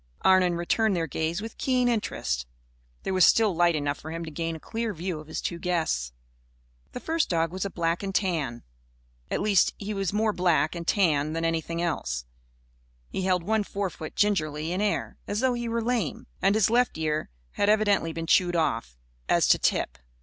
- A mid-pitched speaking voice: Yes, medium, 175 Hz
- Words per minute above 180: Yes, average, 195 wpm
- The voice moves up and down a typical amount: Yes, average, 4.4 semitones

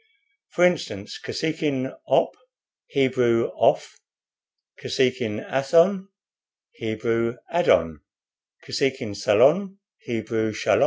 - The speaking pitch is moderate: No, low, 125 Hz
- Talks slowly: Yes, slow, 75 wpm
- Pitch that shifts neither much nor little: No, wide, 6.0 semitones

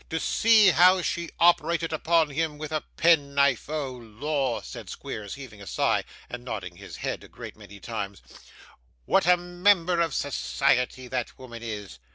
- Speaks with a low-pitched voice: No, medium, 145 Hz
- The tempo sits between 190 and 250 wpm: No, average, 170 wpm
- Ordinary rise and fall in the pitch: No, wide, 6.3 semitones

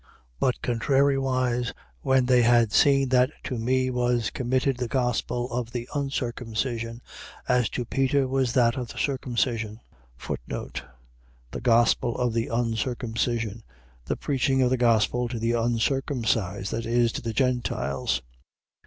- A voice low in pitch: Yes, low, 120 Hz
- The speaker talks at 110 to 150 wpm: Yes, slow, 135 wpm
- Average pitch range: No, narrow, 2.0 semitones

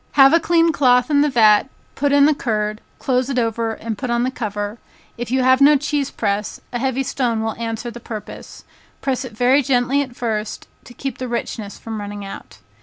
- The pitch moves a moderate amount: Yes, average, 3.5 semitones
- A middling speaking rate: No, fast, 210 wpm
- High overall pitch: Yes, high, 245 Hz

